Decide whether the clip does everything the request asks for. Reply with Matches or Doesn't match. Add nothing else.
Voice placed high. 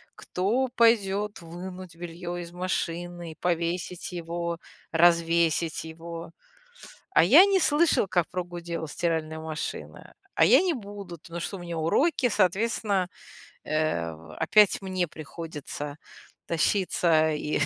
Doesn't match